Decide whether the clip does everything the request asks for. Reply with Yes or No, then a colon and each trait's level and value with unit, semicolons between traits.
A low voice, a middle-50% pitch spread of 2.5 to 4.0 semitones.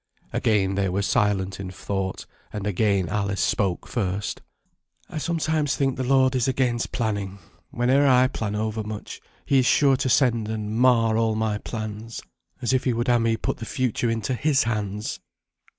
Yes: low, 110 Hz; average, 3.7 semitones